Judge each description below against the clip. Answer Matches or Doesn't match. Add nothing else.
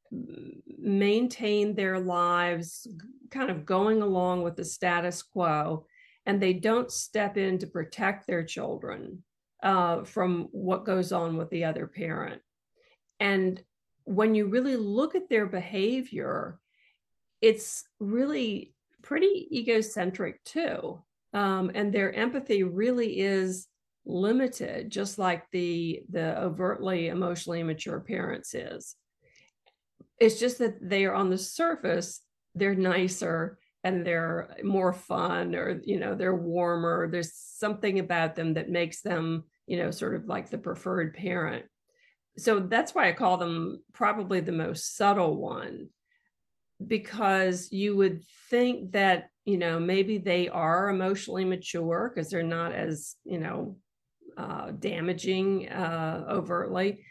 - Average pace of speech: Doesn't match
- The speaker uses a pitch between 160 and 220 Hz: Matches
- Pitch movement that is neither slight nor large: Matches